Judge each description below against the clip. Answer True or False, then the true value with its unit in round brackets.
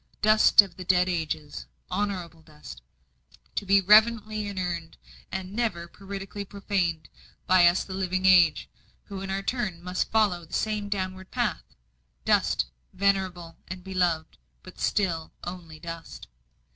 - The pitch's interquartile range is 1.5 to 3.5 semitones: True (2.6 semitones)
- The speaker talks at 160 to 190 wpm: False (135 wpm)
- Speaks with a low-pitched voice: False (185 Hz)